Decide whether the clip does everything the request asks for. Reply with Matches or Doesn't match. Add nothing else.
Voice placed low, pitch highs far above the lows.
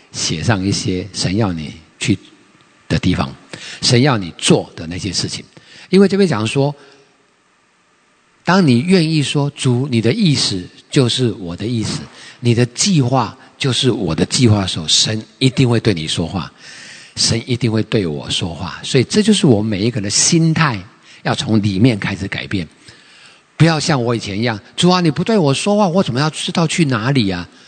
Matches